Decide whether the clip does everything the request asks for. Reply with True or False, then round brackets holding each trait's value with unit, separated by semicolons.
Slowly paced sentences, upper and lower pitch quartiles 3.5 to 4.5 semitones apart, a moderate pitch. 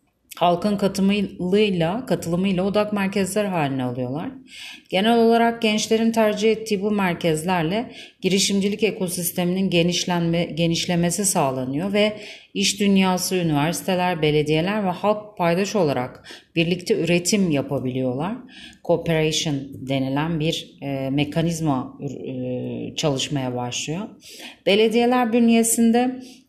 False (90 wpm; 5.2 semitones; 180 Hz)